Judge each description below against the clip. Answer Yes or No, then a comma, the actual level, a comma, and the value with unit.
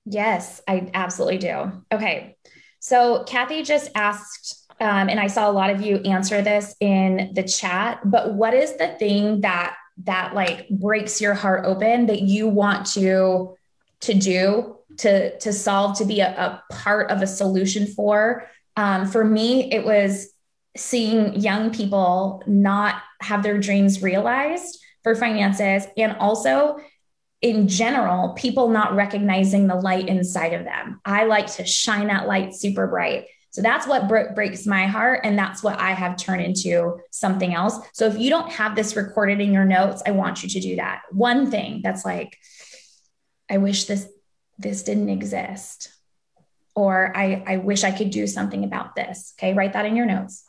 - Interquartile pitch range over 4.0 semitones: No, narrow, 2.4 semitones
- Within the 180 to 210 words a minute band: No, average, 170 wpm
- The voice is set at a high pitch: Yes, high, 200 Hz